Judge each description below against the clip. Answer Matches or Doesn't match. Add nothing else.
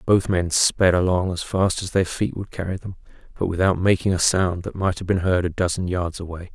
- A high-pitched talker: Doesn't match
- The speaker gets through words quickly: Matches